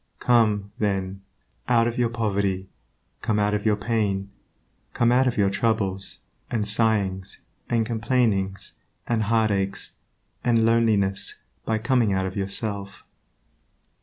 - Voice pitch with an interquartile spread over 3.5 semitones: No, average, 2.8 semitones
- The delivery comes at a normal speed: No, slow, 125 wpm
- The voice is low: Yes, low, 105 Hz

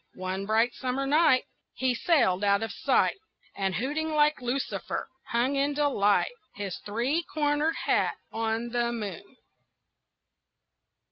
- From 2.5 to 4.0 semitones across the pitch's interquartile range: No, wide, 5.4 semitones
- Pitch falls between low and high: No, high, 245 Hz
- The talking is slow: Yes, slow, 125 wpm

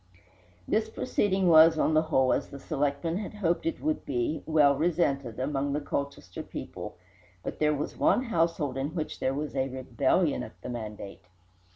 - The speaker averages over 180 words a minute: No, average, 175 wpm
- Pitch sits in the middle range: Yes, medium, 150 Hz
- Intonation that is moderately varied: Yes, average, 3.8 semitones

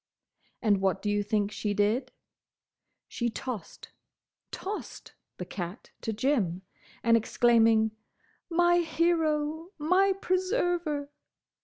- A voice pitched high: Yes, very high, 250 Hz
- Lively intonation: Yes, wide, 8.2 semitones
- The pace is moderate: No, slow, 95 wpm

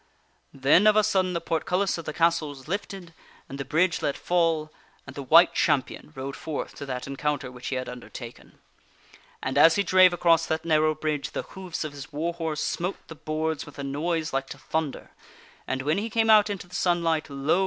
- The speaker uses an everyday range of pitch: Yes, average, 3.7 semitones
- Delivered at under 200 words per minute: No, fast, 205 wpm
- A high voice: No, medium, 160 Hz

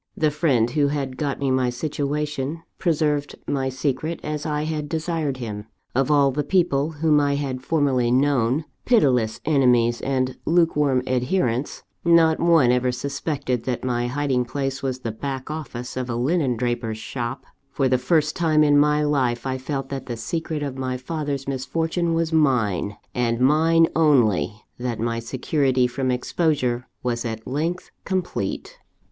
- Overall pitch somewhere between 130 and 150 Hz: Yes, low, 135 Hz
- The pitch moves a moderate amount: Yes, average, 3.4 semitones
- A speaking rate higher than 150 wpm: Yes, average, 160 wpm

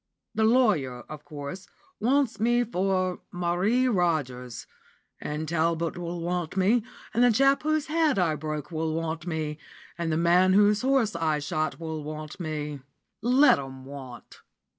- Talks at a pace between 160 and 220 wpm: No, average, 150 wpm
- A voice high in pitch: No, medium, 170 Hz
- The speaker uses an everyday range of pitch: No, wide, 5.8 semitones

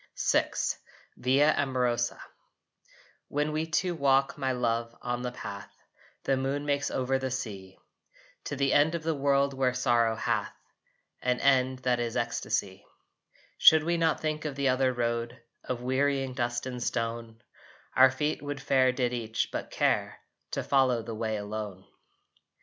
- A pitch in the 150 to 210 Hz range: No, low, 130 Hz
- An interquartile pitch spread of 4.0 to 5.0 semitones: No, average, 2.8 semitones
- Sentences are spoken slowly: No, average, 155 wpm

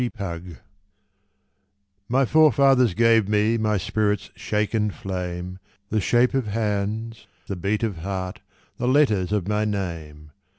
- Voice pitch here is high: No, low, 105 Hz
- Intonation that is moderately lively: Yes, average, 3.6 semitones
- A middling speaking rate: No, slow, 125 wpm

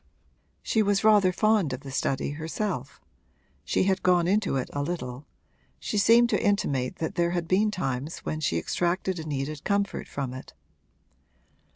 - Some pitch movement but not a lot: No, wide, 6.5 semitones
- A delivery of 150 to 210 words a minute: Yes, average, 165 wpm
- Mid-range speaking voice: Yes, medium, 170 Hz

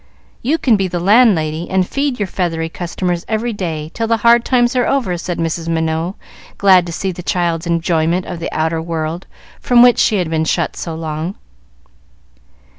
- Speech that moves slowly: No, average, 185 wpm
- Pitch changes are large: No, average, 4.7 semitones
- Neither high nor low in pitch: Yes, medium, 175 Hz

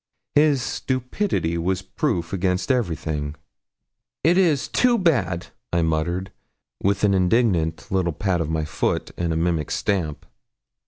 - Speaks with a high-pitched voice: No, very low, 90 Hz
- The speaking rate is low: Yes, slow, 125 wpm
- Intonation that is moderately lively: No, wide, 7.0 semitones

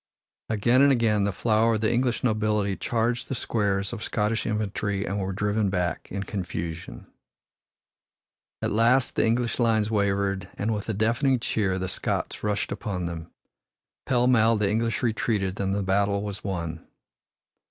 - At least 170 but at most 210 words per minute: No, average, 160 wpm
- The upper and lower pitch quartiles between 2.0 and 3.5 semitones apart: Yes, narrow, 2.6 semitones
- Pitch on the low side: Yes, low, 105 Hz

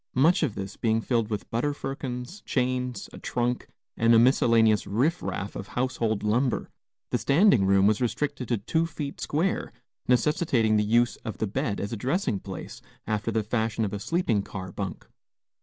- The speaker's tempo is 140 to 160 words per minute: No, average, 175 wpm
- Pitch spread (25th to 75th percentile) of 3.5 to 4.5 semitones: Yes, average, 4.0 semitones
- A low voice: Yes, low, 115 Hz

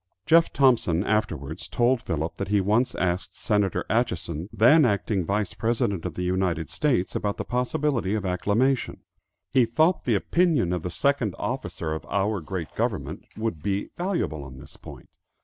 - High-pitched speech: No, low, 100 Hz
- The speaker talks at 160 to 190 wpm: Yes, average, 165 wpm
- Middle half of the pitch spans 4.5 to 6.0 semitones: Yes, wide, 5.5 semitones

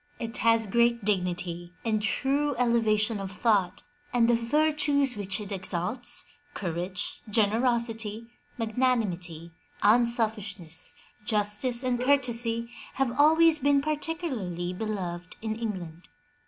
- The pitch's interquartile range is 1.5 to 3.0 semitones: No, average, 4.2 semitones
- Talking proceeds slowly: Yes, slow, 110 wpm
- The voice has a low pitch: No, high, 225 Hz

